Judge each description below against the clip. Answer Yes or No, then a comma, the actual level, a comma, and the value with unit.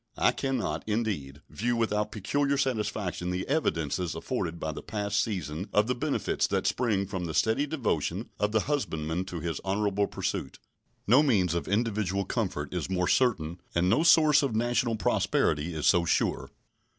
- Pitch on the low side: Yes, low, 100 Hz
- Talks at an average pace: Yes, average, 165 wpm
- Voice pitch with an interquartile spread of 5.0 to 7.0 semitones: Yes, wide, 5.4 semitones